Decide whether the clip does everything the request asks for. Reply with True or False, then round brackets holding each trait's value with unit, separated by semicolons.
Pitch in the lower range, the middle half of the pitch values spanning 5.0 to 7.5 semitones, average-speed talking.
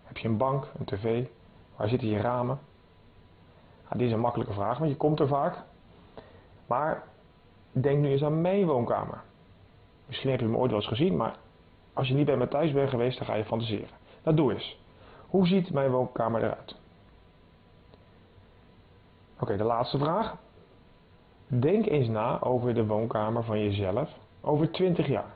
True (115 Hz; 5.6 semitones; 175 wpm)